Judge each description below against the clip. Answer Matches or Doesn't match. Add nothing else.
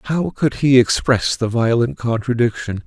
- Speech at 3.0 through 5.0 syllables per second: Matches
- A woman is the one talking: Doesn't match